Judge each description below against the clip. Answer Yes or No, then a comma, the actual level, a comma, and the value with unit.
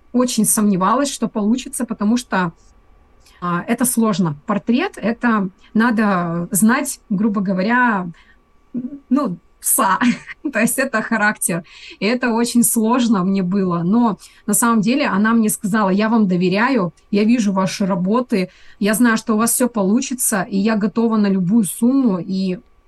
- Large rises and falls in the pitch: No, average, 3.6 semitones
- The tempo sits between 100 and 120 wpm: No, average, 145 wpm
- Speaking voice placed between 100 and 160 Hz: No, high, 220 Hz